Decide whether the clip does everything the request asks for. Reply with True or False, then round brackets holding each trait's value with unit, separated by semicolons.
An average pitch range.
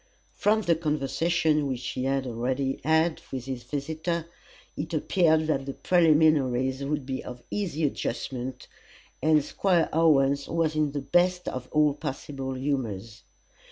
True (3.3 semitones)